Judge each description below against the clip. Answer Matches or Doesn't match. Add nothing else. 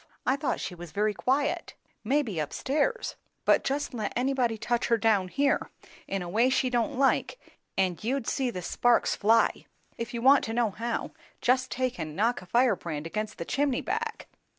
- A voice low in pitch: Doesn't match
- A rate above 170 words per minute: Matches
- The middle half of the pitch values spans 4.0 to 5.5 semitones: Matches